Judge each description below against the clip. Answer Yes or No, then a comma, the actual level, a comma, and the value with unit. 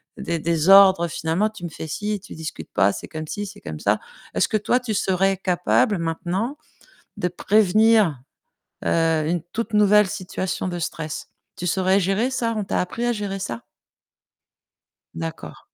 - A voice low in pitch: No, high, 190 Hz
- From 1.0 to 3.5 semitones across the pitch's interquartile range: No, average, 4.1 semitones